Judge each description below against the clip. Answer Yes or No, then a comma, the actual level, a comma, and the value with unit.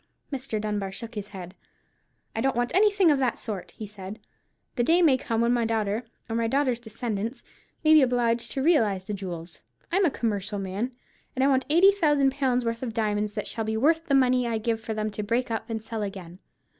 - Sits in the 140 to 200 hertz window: No, high, 230 Hz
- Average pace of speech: No, fast, 220 wpm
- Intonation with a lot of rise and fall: No, average, 3.9 semitones